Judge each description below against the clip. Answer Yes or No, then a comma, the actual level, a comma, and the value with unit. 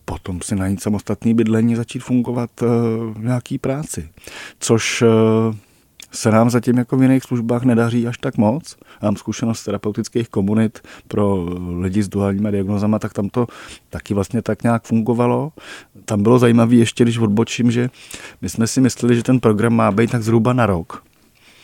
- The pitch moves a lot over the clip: No, narrow, 2.4 semitones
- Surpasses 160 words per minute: Yes, fast, 170 wpm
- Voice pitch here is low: Yes, low, 115 Hz